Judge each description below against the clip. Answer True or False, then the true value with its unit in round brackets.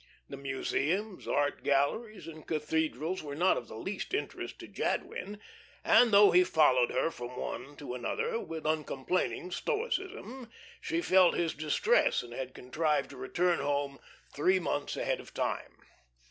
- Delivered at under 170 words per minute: True (150 wpm)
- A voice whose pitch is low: False (160 Hz)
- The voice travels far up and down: True (5.9 semitones)